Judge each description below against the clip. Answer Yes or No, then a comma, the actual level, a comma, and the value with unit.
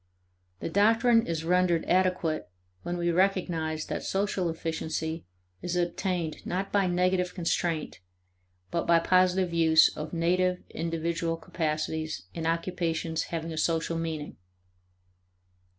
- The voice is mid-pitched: Yes, medium, 170 Hz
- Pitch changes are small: Yes, narrow, 2.0 semitones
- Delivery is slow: Yes, slow, 120 wpm